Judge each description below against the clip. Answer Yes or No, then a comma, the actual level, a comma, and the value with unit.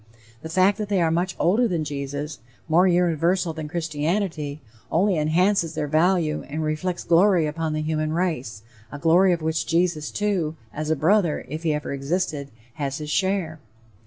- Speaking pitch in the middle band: Yes, medium, 160 Hz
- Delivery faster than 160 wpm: Yes, average, 170 wpm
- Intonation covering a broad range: No, average, 2.9 semitones